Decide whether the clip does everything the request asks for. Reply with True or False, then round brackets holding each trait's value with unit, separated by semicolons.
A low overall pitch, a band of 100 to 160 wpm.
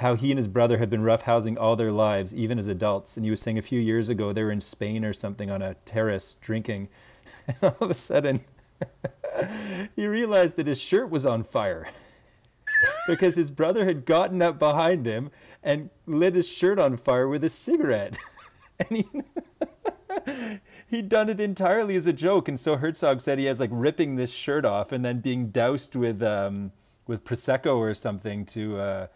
False (130 Hz; 195 wpm)